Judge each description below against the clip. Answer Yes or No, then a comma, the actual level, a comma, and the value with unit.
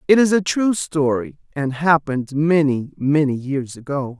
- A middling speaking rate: Yes, average, 155 wpm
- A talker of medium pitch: Yes, medium, 155 Hz